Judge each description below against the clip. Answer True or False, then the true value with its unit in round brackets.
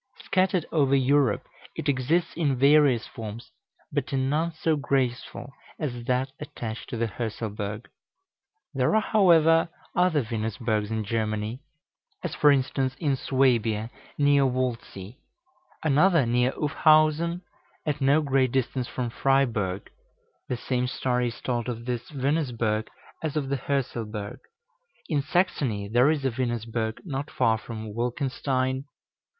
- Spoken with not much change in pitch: False (3.9 semitones)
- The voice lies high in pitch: False (130 Hz)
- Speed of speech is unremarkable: False (130 wpm)